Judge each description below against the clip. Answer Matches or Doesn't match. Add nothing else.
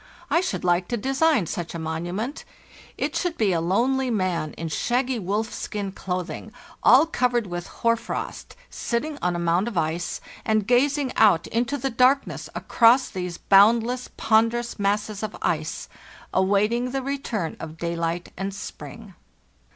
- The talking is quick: Doesn't match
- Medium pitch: Doesn't match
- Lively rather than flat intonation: Matches